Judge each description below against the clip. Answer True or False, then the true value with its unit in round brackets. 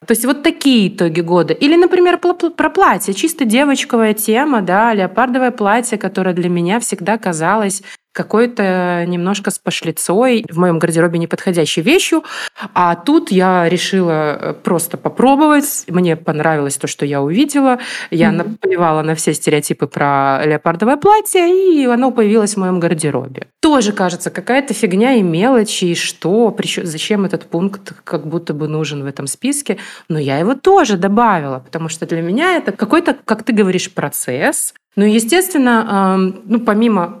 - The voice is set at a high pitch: True (200 Hz)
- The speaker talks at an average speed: True (150 wpm)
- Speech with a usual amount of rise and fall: False (6.7 semitones)